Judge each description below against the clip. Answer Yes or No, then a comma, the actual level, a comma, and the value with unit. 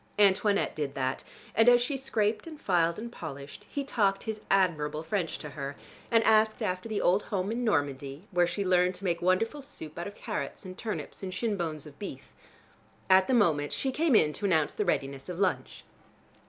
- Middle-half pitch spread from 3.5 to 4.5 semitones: No, wide, 5.6 semitones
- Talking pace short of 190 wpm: No, average, 200 wpm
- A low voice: No, medium, 185 Hz